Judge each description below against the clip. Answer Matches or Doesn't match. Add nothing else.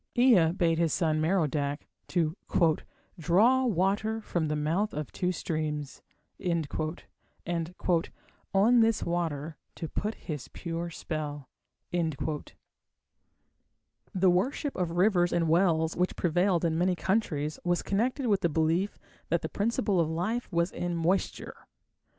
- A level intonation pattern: Doesn't match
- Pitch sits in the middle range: Matches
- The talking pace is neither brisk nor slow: Doesn't match